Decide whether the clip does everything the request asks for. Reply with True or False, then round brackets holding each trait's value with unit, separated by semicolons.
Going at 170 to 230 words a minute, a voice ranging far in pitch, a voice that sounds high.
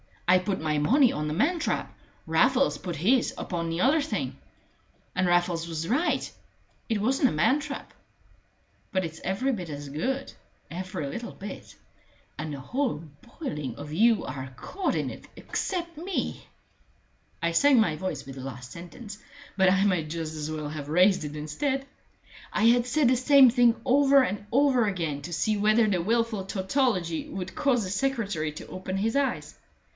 True (175 wpm; 7.9 semitones; 195 Hz)